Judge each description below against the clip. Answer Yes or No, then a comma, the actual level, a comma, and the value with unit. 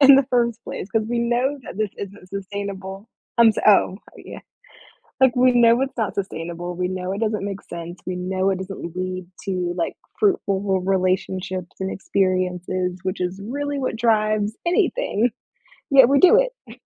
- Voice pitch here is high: Yes, high, 200 Hz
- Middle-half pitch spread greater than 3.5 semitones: Yes, average, 4.3 semitones